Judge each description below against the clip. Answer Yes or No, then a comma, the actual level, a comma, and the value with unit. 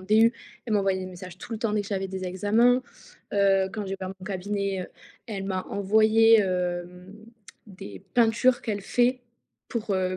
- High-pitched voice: Yes, high, 200 Hz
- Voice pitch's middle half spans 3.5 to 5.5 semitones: No, average, 2.8 semitones